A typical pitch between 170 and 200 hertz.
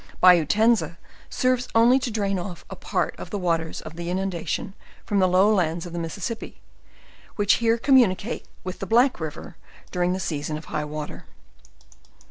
Yes: medium, 185 Hz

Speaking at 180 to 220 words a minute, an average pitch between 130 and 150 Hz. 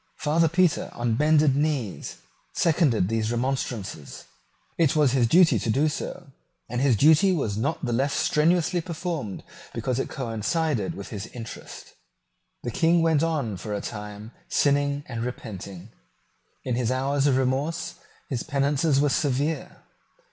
No: average, 145 wpm; low, 135 Hz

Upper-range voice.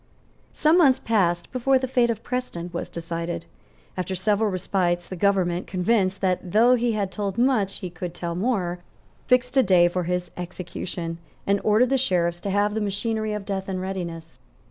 Yes: high, 195 Hz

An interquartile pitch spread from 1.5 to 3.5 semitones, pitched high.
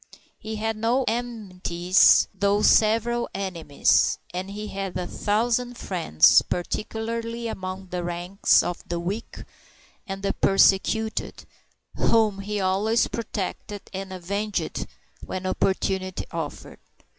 Yes: average, 3.0 semitones; high, 200 Hz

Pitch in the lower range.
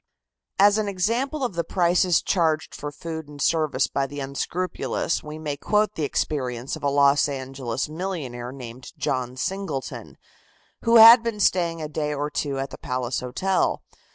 No: medium, 150 Hz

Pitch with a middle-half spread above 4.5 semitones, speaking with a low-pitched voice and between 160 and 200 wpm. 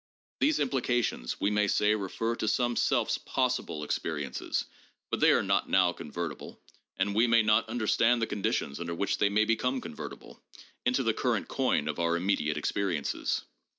Yes: average, 5.1 semitones; low, 100 Hz; average, 170 wpm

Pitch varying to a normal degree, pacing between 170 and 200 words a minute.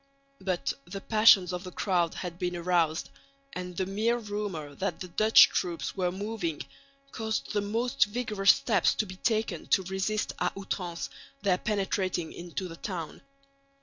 No: average, 3.1 semitones; average, 155 wpm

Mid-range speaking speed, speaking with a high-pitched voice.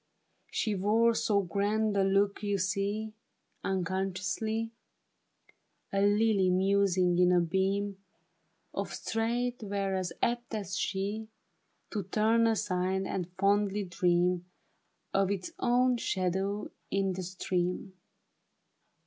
No: slow, 110 wpm; high, 195 Hz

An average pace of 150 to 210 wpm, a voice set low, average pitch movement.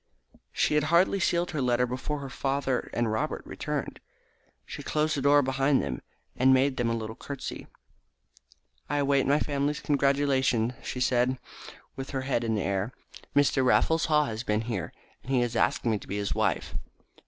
Yes: average, 180 wpm; low, 130 Hz; average, 3.4 semitones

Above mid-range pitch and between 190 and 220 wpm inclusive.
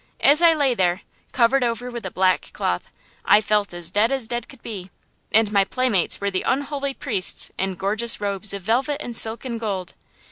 Yes: high, 225 Hz; average, 200 wpm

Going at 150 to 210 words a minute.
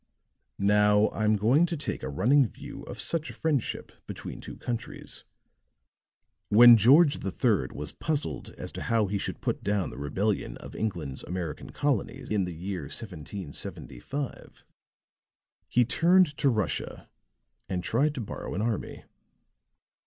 No: average, 140 wpm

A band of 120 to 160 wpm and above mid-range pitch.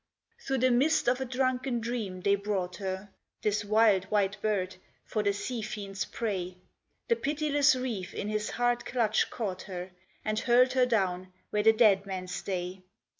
No: average, 170 wpm; high, 210 Hz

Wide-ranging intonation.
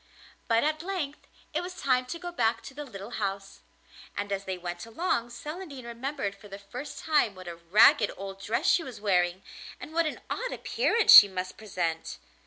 Yes: wide, 7.4 semitones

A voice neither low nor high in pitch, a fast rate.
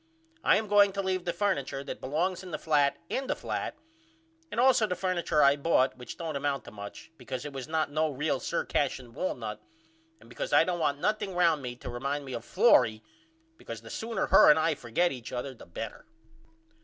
Yes: medium, 150 Hz; fast, 210 wpm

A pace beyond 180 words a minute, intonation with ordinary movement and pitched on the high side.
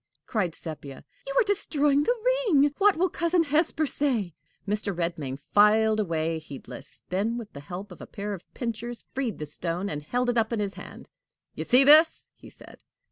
No: average, 190 wpm; wide, 8.7 semitones; high, 220 Hz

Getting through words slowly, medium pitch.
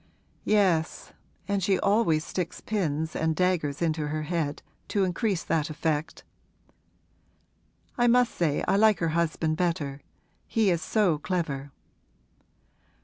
Yes: slow, 125 wpm; medium, 170 Hz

